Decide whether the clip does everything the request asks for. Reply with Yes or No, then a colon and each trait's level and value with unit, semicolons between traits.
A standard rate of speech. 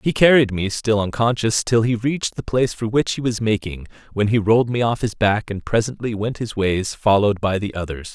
No: fast, 230 wpm